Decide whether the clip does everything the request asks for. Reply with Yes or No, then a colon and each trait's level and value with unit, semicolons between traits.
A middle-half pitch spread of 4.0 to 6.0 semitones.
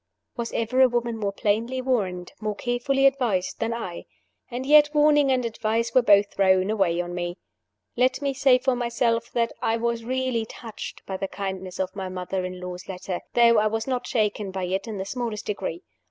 Yes: average, 4.6 semitones